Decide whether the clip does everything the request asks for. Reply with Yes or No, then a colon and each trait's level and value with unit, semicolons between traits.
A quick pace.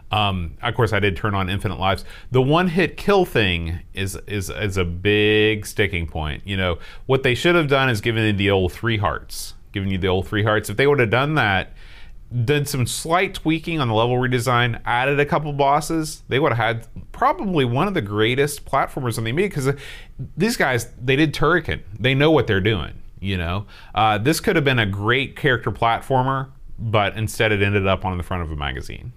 Yes: fast, 215 wpm